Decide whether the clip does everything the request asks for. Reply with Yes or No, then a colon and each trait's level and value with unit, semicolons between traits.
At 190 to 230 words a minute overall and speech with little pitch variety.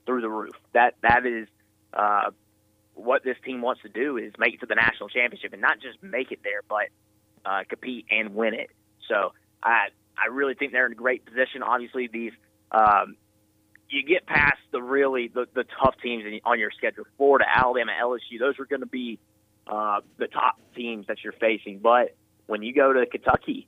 No: average, 200 wpm; average, 3.2 semitones